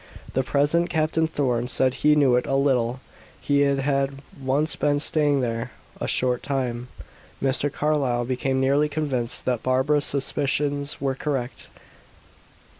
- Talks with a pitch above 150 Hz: No, low, 135 Hz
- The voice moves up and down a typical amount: No, narrow, 2.3 semitones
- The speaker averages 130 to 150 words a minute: Yes, slow, 135 wpm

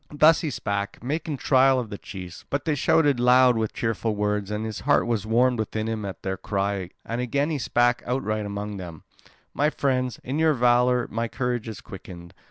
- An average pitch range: Yes, average, 3.9 semitones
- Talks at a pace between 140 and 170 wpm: No, average, 195 wpm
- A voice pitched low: Yes, low, 115 Hz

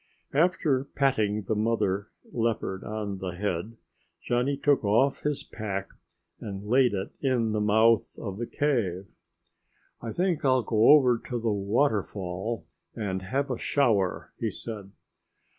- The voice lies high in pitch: No, low, 110 Hz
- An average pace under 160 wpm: Yes, average, 140 wpm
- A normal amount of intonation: Yes, average, 4.4 semitones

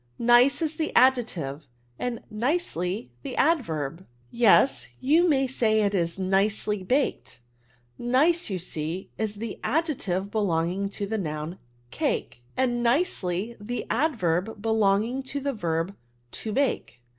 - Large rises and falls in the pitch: Yes, wide, 6.0 semitones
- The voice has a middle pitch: No, high, 215 Hz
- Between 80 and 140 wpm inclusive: Yes, slow, 135 wpm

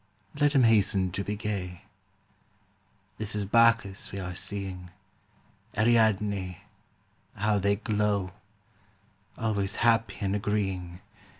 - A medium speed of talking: No, slow, 115 wpm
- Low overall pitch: Yes, low, 100 Hz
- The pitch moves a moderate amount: No, narrow, 2.2 semitones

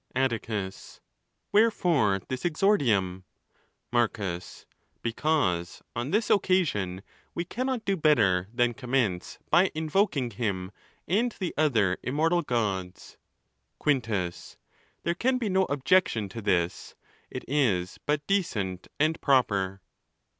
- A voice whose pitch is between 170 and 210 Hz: No, low, 125 Hz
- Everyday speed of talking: No, slow, 105 wpm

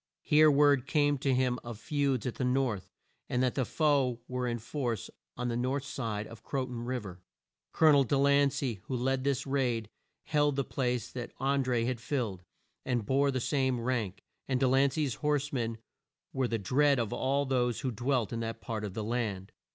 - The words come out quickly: Yes, fast, 210 wpm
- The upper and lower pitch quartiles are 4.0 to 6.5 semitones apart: No, average, 2.9 semitones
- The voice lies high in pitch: No, low, 130 Hz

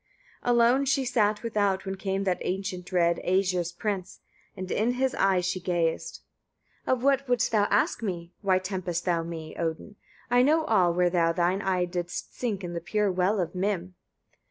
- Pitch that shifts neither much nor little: Yes, average, 3.3 semitones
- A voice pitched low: No, high, 190 Hz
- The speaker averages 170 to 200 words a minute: Yes, average, 185 wpm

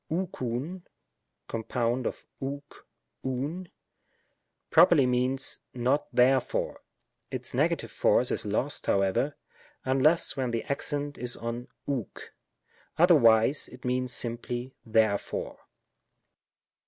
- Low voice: Yes, low, 130 Hz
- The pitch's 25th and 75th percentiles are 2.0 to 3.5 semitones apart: Yes, average, 3.1 semitones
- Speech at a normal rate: No, slow, 100 wpm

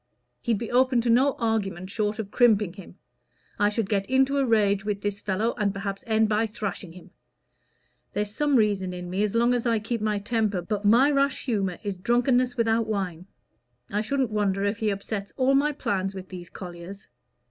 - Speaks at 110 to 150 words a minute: No, average, 195 wpm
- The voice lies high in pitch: Yes, high, 210 Hz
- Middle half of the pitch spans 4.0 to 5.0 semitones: No, average, 3.2 semitones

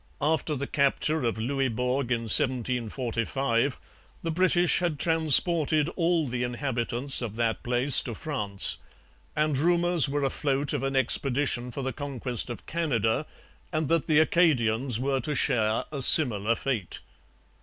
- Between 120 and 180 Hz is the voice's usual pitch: Yes, low, 135 Hz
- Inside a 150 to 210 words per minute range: No, average, 140 wpm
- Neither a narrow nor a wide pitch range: Yes, average, 4.1 semitones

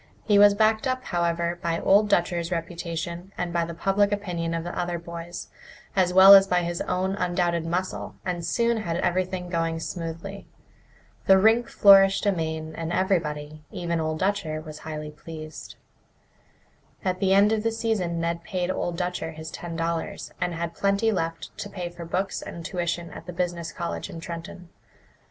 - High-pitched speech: No, medium, 175 Hz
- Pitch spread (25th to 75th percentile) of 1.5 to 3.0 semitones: Yes, narrow, 2.5 semitones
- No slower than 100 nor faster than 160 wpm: No, average, 175 wpm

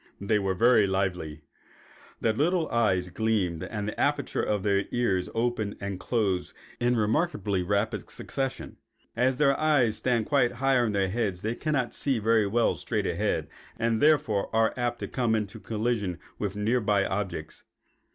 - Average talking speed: Yes, average, 160 wpm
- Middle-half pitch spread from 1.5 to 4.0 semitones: Yes, average, 3.6 semitones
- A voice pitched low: Yes, low, 110 Hz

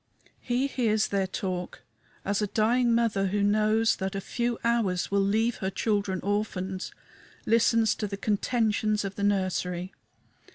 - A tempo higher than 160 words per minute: No, average, 150 wpm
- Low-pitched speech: No, high, 205 Hz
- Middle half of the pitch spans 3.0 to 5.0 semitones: No, narrow, 2.6 semitones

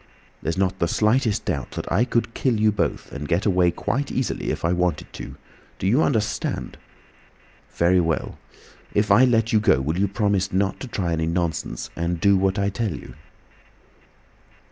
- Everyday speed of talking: Yes, average, 175 wpm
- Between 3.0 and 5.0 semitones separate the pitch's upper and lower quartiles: Yes, average, 4.1 semitones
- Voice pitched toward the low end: Yes, very low, 95 Hz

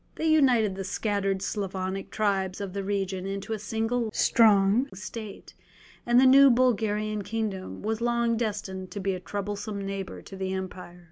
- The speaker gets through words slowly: No, average, 160 wpm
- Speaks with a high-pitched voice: Yes, high, 205 Hz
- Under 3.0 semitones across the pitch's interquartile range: Yes, narrow, 2.6 semitones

